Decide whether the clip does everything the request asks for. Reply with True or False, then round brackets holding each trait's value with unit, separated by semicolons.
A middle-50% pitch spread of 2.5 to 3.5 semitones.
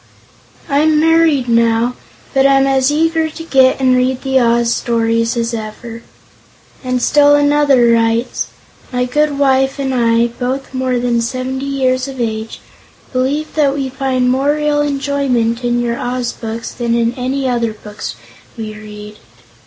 True (2.9 semitones)